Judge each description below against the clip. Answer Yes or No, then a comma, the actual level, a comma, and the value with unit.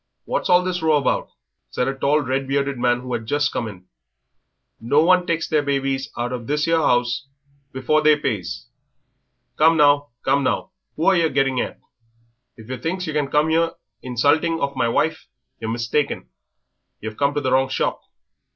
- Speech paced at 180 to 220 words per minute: Yes, average, 185 wpm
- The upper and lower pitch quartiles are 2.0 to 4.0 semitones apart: Yes, average, 3.7 semitones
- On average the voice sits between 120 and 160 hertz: Yes, medium, 140 Hz